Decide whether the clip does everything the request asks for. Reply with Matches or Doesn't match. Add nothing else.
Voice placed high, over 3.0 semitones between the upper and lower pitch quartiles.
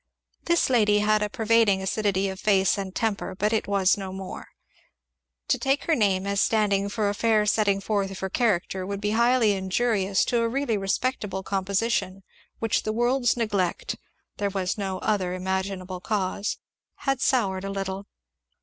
Doesn't match